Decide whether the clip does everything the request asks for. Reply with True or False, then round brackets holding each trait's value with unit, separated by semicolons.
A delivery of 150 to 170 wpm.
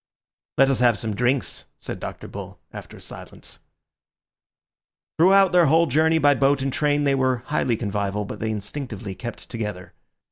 True (165 wpm)